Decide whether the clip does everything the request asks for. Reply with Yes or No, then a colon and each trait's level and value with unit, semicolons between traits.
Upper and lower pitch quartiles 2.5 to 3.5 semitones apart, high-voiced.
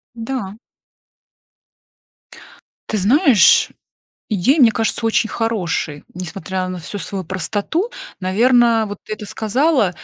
No: average, 4.1 semitones; high, 215 Hz